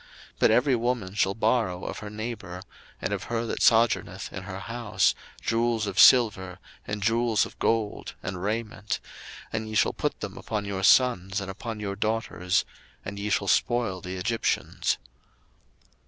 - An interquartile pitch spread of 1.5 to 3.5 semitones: Yes, average, 3.1 semitones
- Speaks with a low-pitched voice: Yes, low, 105 Hz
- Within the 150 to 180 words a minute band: Yes, average, 165 wpm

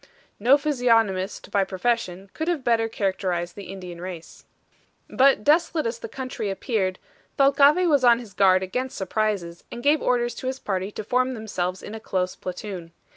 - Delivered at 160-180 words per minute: Yes, average, 170 wpm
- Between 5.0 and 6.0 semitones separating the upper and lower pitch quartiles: Yes, wide, 5.4 semitones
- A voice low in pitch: No, high, 215 Hz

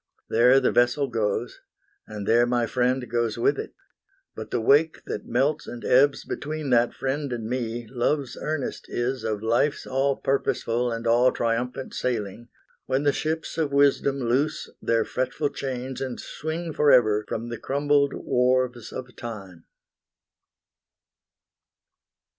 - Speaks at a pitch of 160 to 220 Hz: No, low, 125 Hz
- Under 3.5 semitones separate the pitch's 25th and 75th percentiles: Yes, average, 2.9 semitones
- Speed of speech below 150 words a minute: Yes, average, 140 wpm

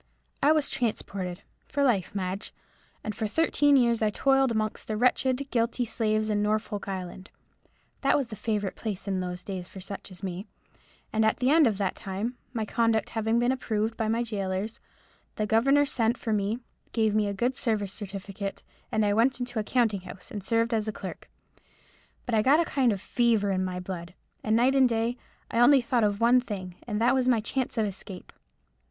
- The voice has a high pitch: Yes, high, 220 Hz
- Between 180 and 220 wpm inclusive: Yes, average, 200 wpm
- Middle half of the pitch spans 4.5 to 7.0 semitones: No, average, 3.3 semitones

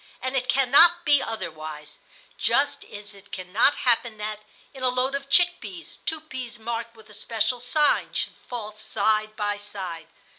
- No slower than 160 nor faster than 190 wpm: Yes, average, 170 wpm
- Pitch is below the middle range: No, high, 230 Hz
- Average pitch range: Yes, average, 4.5 semitones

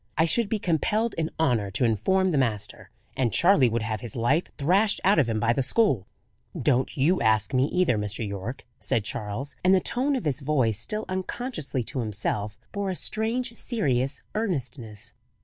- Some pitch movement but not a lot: No, wide, 8.8 semitones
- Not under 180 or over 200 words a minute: Yes, average, 185 wpm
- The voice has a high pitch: No, low, 135 Hz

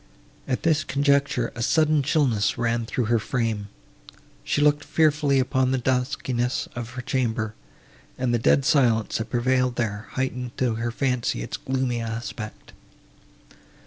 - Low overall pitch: Yes, low, 125 Hz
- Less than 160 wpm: Yes, average, 145 wpm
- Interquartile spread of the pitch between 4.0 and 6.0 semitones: No, average, 2.8 semitones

